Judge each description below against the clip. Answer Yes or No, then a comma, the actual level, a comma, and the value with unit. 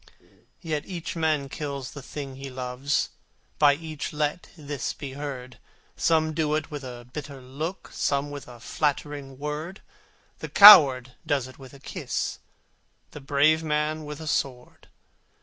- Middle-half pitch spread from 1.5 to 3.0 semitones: Yes, narrow, 2.4 semitones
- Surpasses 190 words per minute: No, average, 150 wpm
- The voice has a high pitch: No, medium, 145 Hz